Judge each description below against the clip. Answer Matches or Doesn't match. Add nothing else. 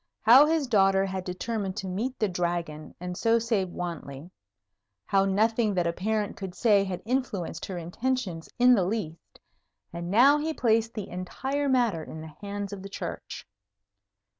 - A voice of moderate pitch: Doesn't match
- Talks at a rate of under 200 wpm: Matches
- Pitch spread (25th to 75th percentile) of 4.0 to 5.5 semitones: Matches